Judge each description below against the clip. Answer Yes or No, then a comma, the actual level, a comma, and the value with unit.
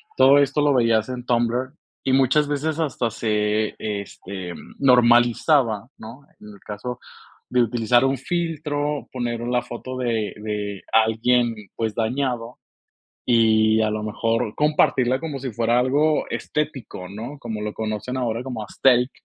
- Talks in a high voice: No, low, 120 Hz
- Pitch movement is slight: No, average, 3.3 semitones